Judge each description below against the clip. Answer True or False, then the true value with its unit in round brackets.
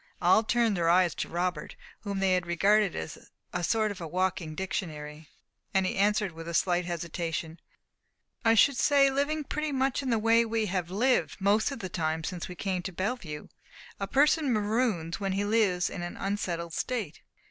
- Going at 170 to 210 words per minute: True (180 wpm)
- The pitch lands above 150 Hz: True (190 Hz)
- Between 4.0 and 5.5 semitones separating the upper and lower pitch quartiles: True (4.6 semitones)